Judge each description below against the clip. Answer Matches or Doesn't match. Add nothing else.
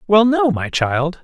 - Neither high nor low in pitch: Matches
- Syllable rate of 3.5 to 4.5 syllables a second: Matches